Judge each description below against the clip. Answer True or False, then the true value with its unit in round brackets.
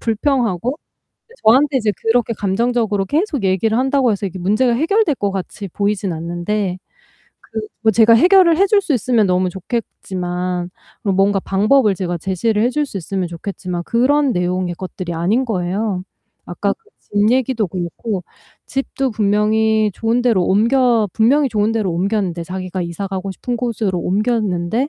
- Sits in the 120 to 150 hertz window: False (210 Hz)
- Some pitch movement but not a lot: True (4.6 semitones)